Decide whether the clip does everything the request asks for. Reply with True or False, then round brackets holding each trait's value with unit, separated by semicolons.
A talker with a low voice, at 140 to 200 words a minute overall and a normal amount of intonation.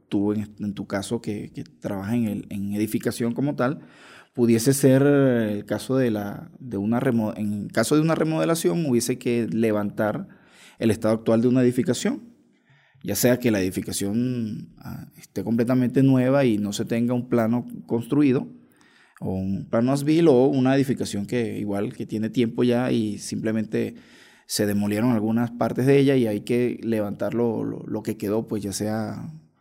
True (115 Hz; 170 wpm; 3.2 semitones)